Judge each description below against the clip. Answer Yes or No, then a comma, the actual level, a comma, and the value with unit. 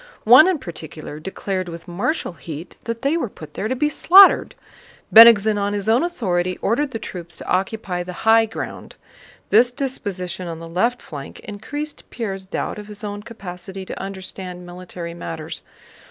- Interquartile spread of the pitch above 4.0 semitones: Yes, average, 4.6 semitones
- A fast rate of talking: No, average, 170 wpm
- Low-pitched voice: No, high, 195 Hz